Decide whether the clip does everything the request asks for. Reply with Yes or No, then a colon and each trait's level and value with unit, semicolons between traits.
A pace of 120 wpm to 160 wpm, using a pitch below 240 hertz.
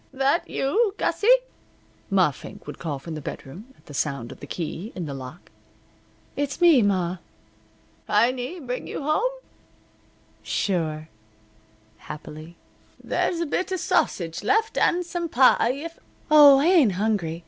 No: average, 150 wpm; high, 245 Hz